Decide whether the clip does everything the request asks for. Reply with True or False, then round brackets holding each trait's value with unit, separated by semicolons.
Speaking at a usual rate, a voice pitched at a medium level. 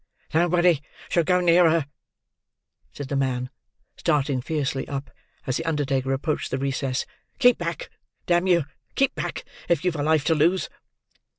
True (155 wpm; 155 Hz)